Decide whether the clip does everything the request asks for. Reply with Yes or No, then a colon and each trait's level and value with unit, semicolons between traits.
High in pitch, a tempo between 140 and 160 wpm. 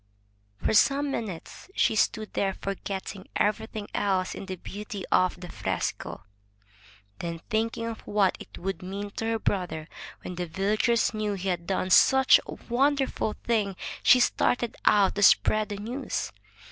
Yes: high, 205 Hz; average, 155 wpm